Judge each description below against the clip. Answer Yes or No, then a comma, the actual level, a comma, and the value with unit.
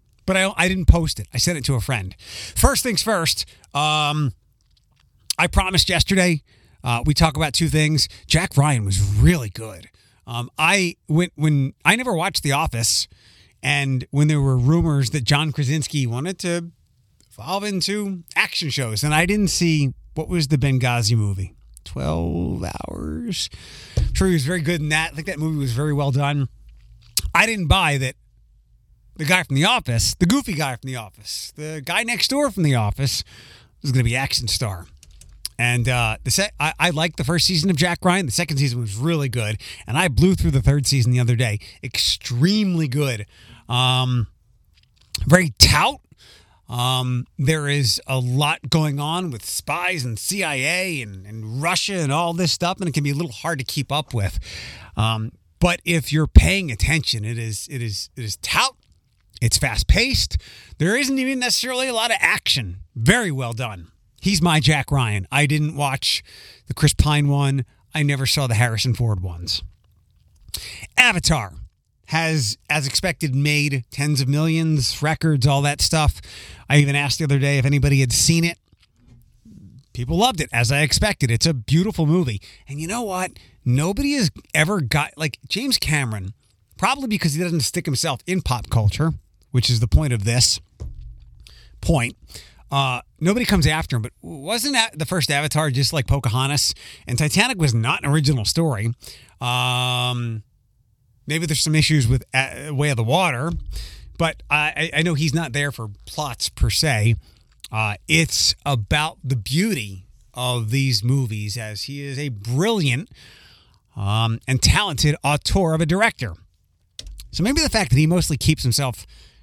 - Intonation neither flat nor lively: No, wide, 6.1 semitones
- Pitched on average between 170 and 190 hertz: No, low, 135 Hz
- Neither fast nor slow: Yes, average, 175 wpm